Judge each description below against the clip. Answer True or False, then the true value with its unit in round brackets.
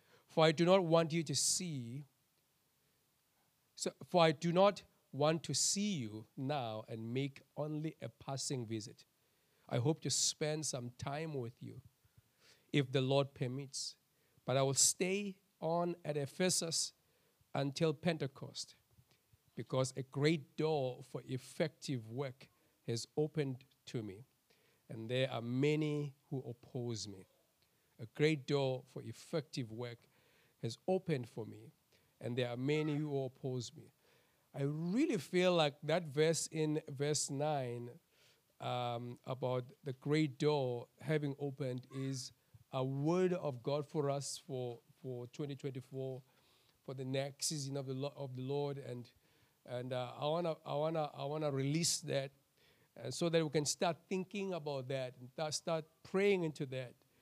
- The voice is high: False (140 Hz)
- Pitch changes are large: False (3.2 semitones)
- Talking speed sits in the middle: True (150 wpm)